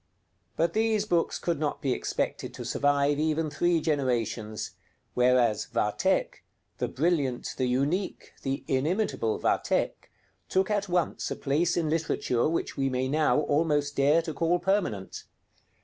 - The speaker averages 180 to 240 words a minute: No, average, 140 wpm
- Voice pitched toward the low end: No, medium, 150 Hz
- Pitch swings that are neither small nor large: Yes, average, 4.3 semitones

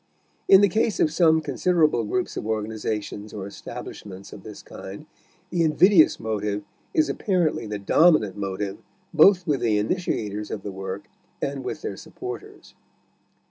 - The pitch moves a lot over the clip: Yes, wide, 8.3 semitones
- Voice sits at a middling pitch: No, low, 110 Hz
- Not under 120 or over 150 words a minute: Yes, average, 145 wpm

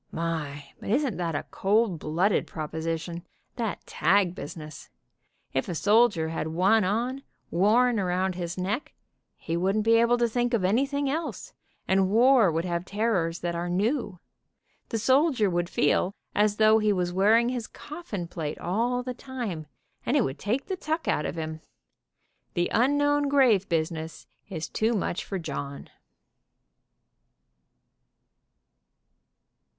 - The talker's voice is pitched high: Yes, high, 200 Hz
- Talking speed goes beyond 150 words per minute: No, average, 145 wpm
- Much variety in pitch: Yes, wide, 5.9 semitones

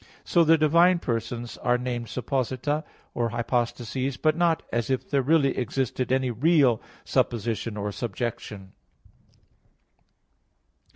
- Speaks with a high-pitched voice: No, low, 125 Hz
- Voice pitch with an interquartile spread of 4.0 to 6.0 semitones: No, average, 3.6 semitones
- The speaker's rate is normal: No, slow, 115 wpm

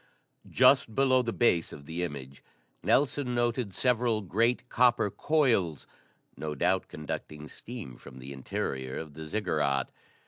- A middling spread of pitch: No, wide, 8.3 semitones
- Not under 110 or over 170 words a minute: Yes, slow, 135 wpm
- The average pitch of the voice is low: Yes, very low, 95 Hz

